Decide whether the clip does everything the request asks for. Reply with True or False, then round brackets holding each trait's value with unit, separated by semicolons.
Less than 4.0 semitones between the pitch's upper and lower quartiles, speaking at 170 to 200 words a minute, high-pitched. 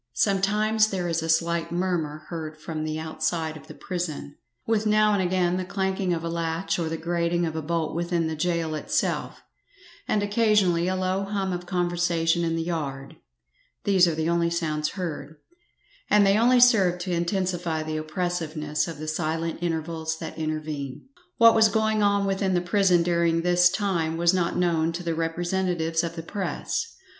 False (2.6 semitones; 180 wpm; 170 Hz)